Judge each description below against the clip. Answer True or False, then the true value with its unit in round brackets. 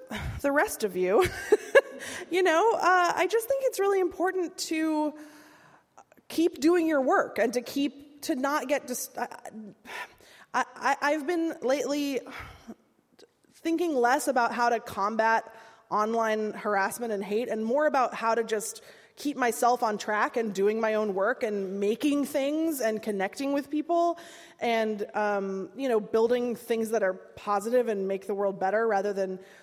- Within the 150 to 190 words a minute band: True (160 wpm)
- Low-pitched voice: False (245 Hz)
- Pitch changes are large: True (6.3 semitones)